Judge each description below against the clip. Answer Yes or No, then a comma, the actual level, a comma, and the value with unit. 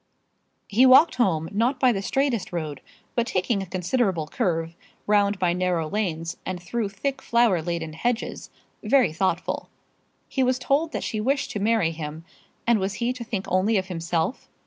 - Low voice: No, high, 195 Hz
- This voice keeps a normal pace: Yes, average, 170 wpm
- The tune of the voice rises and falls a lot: Yes, wide, 5.8 semitones